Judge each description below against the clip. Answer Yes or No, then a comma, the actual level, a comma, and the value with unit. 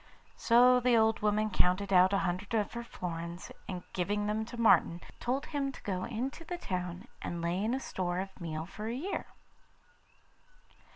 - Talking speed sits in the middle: Yes, average, 180 wpm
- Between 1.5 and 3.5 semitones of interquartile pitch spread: No, average, 4.7 semitones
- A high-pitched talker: Yes, high, 205 Hz